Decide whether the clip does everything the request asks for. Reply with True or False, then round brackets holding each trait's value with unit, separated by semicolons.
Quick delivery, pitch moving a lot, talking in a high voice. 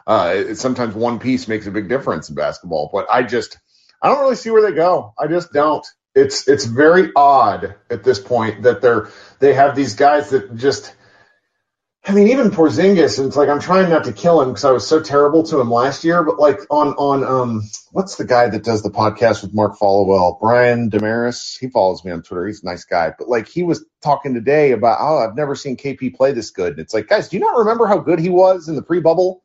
False (240 wpm; 7.4 semitones; 140 Hz)